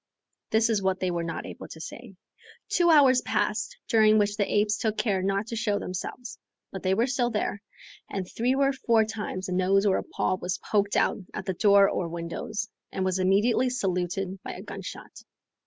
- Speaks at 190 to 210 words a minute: Yes, fast, 205 wpm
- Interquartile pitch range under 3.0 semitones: No, average, 3.3 semitones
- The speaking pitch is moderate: No, high, 205 Hz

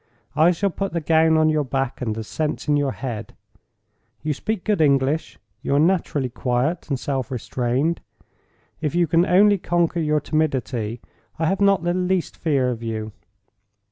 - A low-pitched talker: No, medium, 150 Hz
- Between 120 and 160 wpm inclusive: No, average, 170 wpm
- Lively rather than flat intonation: No, average, 4.7 semitones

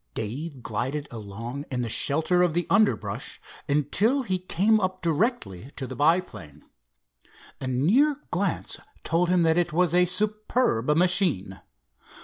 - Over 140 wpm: No, slow, 135 wpm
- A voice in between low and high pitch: Yes, medium, 165 Hz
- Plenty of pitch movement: Yes, wide, 6.3 semitones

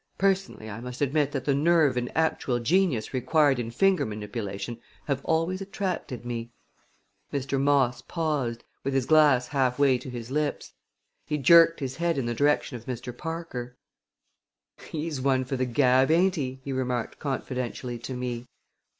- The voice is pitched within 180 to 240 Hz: No, low, 135 Hz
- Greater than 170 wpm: No, average, 160 wpm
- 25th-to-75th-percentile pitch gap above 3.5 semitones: Yes, average, 3.9 semitones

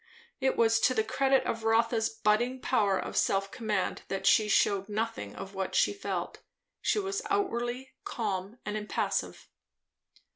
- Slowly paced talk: No, average, 150 wpm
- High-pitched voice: Yes, high, 225 Hz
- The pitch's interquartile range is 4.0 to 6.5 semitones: No, average, 3.6 semitones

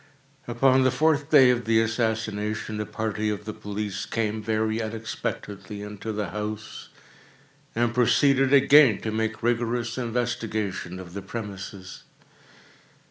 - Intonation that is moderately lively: No, narrow, 2.3 semitones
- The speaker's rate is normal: No, slow, 130 wpm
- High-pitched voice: No, low, 110 Hz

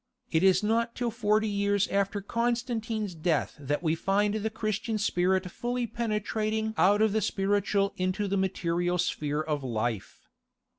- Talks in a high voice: Yes, high, 200 Hz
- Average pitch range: Yes, average, 3.5 semitones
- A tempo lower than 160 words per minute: Yes, average, 150 wpm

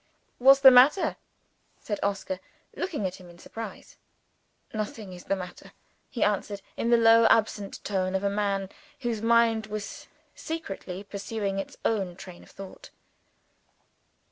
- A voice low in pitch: No, high, 205 Hz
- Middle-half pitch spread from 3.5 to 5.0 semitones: No, average, 2.8 semitones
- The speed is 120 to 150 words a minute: Yes, average, 140 wpm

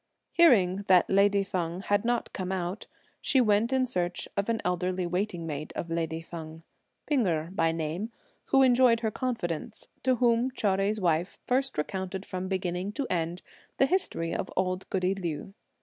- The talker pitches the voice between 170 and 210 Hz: Yes, high, 190 Hz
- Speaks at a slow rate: No, average, 170 wpm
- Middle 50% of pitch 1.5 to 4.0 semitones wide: No, average, 4.9 semitones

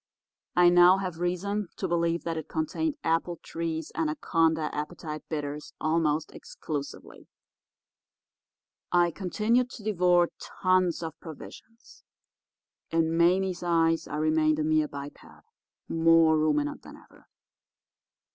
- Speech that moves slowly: Yes, slow, 110 wpm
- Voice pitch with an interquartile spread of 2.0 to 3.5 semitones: Yes, narrow, 2.4 semitones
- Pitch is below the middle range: No, medium, 165 Hz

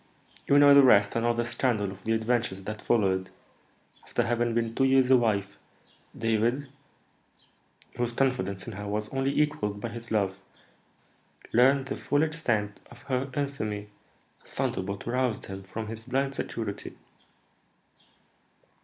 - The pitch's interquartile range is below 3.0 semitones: No, average, 4.1 semitones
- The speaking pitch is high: No, low, 115 Hz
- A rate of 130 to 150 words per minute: Yes, average, 145 wpm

